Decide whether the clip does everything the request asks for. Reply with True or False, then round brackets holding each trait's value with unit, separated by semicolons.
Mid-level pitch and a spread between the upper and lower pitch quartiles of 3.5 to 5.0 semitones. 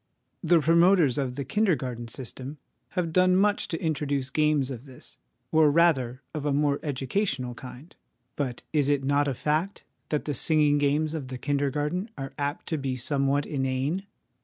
False (145 Hz; 3.1 semitones)